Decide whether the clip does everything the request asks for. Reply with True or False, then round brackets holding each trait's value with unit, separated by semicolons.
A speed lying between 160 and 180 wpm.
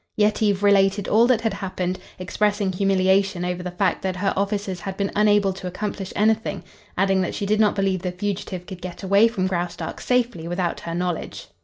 False (190 wpm)